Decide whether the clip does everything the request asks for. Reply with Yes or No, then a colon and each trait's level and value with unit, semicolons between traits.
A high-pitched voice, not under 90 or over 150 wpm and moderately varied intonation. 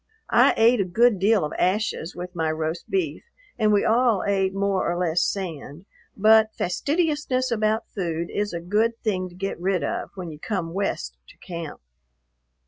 No: high, 195 Hz; average, 175 wpm; average, 4.1 semitones